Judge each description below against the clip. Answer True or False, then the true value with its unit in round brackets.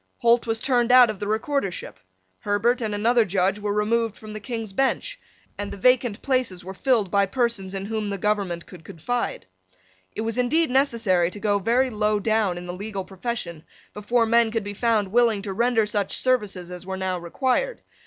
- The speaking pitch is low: False (215 Hz)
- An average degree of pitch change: True (3.5 semitones)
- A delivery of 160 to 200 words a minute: True (195 wpm)